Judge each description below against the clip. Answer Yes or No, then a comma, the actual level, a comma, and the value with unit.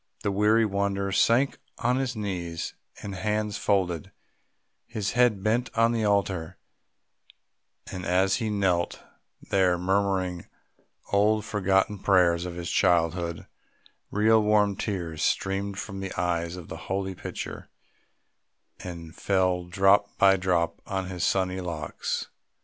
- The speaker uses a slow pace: Yes, slow, 125 wpm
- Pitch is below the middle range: Yes, very low, 95 Hz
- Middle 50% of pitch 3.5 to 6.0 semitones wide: No, narrow, 2.6 semitones